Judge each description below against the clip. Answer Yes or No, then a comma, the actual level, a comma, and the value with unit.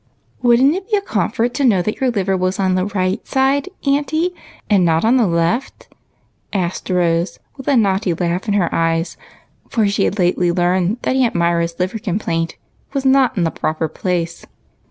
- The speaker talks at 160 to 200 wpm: Yes, average, 195 wpm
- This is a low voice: No, high, 190 Hz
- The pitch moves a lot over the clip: Yes, wide, 6.1 semitones